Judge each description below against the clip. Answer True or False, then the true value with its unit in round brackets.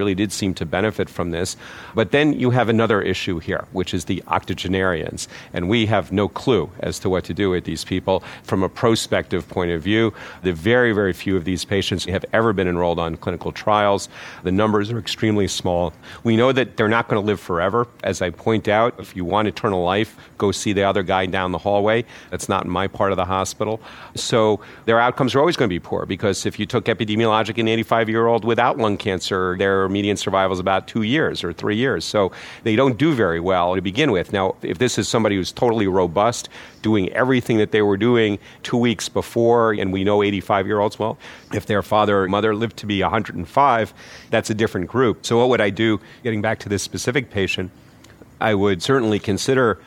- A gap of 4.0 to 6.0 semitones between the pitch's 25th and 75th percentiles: False (3.1 semitones)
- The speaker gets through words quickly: True (220 wpm)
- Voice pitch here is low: True (105 Hz)